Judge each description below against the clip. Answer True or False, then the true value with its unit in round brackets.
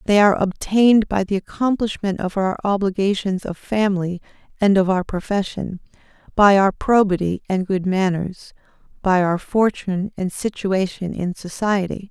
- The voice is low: False (195 Hz)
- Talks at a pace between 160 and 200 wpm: False (140 wpm)